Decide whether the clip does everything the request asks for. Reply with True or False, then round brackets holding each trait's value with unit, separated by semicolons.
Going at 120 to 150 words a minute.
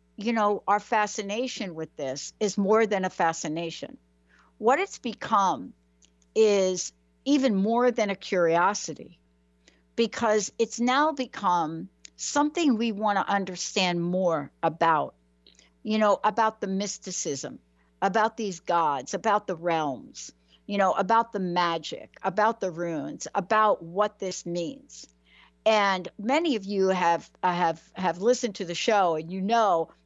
True (135 wpm)